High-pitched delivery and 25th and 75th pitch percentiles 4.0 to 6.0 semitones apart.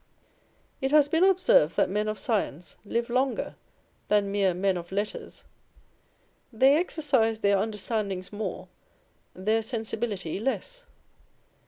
Yes: high, 220 Hz; average, 5.1 semitones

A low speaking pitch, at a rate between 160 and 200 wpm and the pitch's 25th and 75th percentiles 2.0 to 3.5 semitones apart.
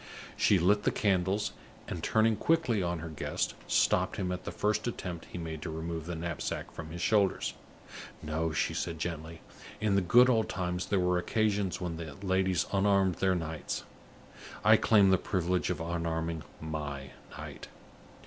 Yes: very low, 90 Hz; average, 170 wpm; average, 3.2 semitones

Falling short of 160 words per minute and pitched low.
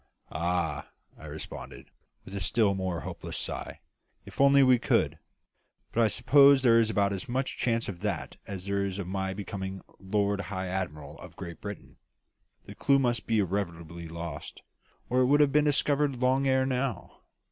No: average, 175 wpm; low, 100 Hz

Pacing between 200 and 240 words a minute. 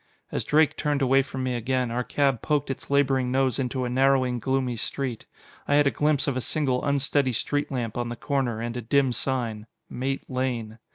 Yes: fast, 205 wpm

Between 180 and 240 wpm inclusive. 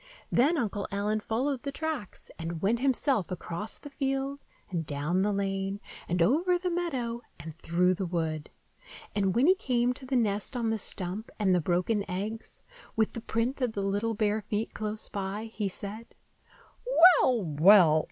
No: average, 170 wpm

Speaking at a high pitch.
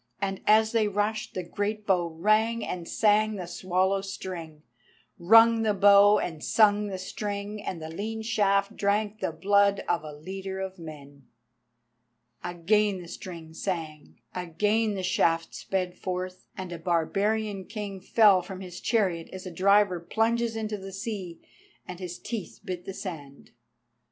Yes: high, 195 Hz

